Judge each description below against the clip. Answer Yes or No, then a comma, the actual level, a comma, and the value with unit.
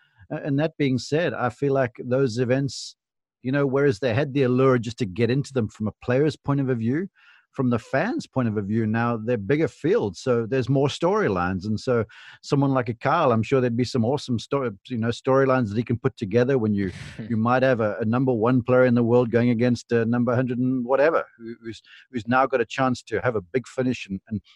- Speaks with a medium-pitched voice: No, low, 125 Hz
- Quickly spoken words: Yes, fast, 230 wpm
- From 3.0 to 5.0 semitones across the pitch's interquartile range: No, narrow, 2.4 semitones